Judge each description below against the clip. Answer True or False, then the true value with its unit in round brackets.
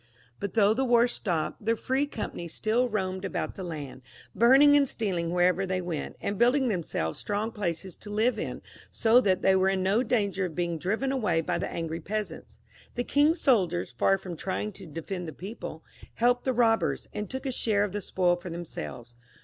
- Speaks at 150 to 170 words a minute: False (200 wpm)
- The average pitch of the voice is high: True (195 Hz)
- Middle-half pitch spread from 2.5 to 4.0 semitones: False (5.0 semitones)